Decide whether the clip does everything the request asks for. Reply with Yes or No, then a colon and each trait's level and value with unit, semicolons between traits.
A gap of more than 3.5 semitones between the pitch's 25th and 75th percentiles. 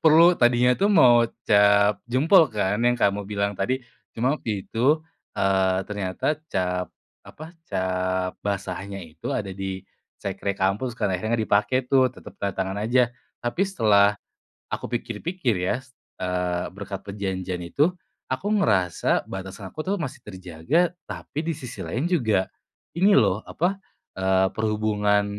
Yes: average, 4.3 semitones